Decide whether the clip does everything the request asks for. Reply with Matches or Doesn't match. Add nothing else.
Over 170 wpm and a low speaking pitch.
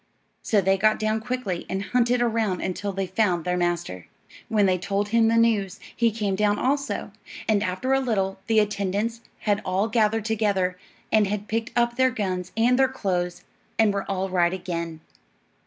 Doesn't match